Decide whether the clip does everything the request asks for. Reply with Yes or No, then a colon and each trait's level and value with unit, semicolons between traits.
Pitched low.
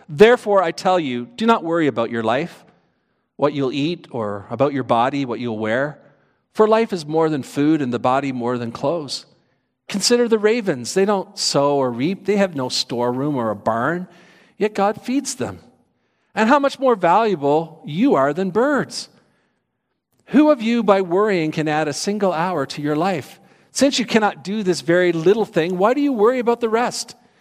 No: medium, 175 Hz